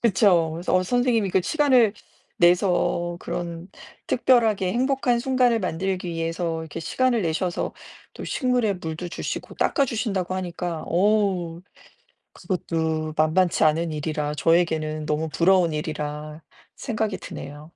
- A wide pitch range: No, average, 4.9 semitones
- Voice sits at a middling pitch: Yes, medium, 175 Hz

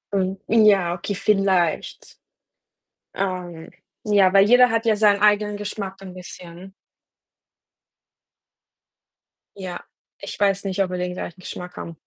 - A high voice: Yes, high, 195 Hz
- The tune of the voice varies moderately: No, narrow, 2.3 semitones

